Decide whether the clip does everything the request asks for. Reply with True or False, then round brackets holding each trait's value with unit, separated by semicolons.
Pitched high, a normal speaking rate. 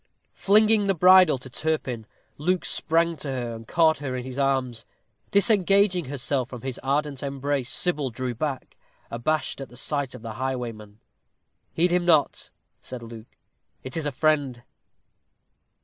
False (140 Hz; 150 wpm)